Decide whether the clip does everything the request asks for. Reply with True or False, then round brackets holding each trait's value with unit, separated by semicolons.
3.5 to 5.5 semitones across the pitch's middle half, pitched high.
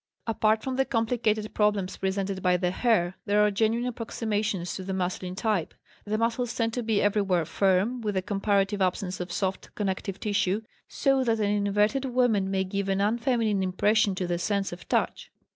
False (2.8 semitones; 205 Hz)